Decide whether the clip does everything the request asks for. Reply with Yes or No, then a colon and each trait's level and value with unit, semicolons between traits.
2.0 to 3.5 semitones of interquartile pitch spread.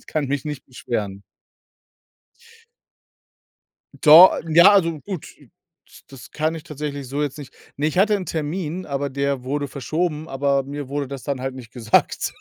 Yes: average, 2.7 semitones